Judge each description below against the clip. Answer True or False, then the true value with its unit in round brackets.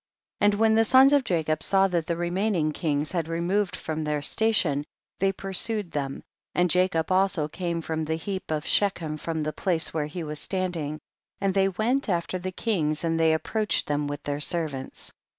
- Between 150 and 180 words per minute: False (205 wpm)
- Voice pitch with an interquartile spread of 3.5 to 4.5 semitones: True (3.9 semitones)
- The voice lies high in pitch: False (170 Hz)